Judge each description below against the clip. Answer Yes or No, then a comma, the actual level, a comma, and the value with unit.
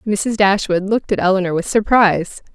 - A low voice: No, high, 195 Hz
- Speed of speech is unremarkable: Yes, average, 165 wpm